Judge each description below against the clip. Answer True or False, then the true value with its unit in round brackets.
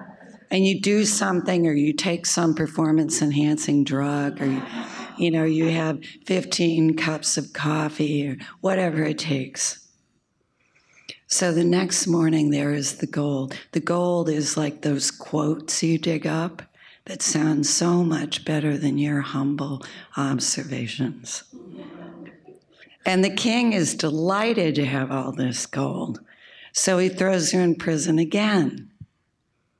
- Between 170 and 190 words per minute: False (135 wpm)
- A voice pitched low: False (155 Hz)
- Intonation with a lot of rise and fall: False (3.2 semitones)